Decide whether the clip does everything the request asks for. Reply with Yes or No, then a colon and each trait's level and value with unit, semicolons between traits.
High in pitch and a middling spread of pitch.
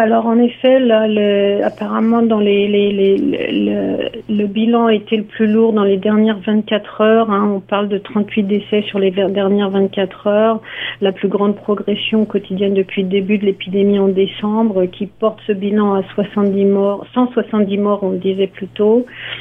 No: high, 205 Hz; narrow, 1.7 semitones